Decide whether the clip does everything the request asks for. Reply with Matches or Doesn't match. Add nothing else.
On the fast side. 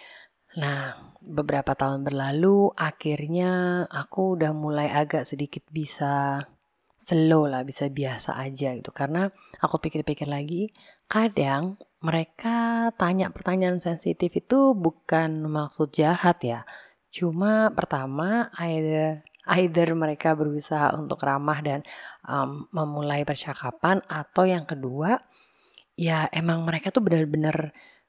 Doesn't match